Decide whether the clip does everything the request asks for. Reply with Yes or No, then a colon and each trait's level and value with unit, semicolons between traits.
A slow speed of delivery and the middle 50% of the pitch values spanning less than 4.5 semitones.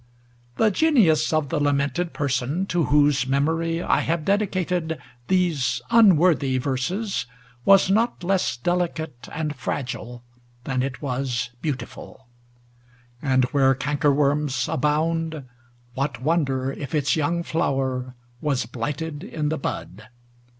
Yes: slow, 115 wpm; average, 4.0 semitones